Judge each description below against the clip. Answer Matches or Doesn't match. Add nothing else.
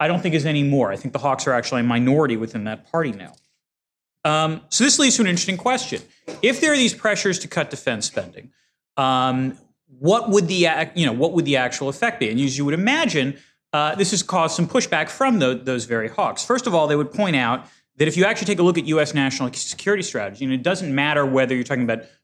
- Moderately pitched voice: Matches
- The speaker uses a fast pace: Matches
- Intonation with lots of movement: Matches